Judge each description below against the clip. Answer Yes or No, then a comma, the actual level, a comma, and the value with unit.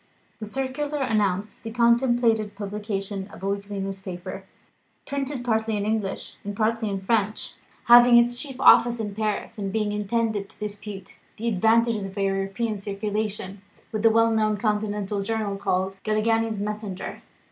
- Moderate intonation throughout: No, narrow, 2.3 semitones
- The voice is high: Yes, high, 215 Hz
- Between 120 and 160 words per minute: Yes, average, 150 wpm